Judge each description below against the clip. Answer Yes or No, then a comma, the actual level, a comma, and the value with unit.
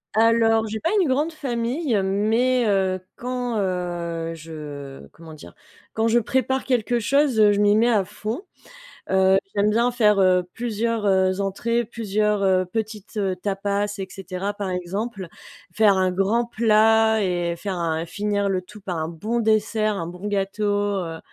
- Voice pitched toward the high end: Yes, high, 205 Hz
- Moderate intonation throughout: Yes, average, 3.4 semitones